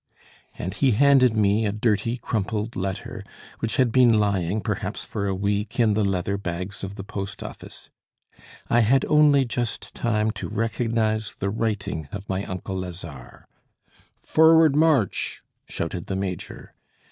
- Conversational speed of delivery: Yes, average, 145 wpm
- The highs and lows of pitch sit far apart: No, average, 3.2 semitones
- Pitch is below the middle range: Yes, low, 105 Hz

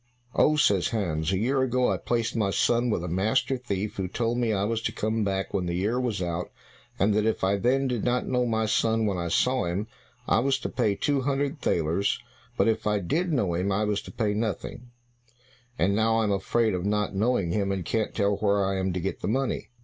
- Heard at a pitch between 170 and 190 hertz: No, low, 105 Hz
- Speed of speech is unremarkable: No, fast, 235 wpm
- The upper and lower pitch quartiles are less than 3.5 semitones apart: No, average, 3.8 semitones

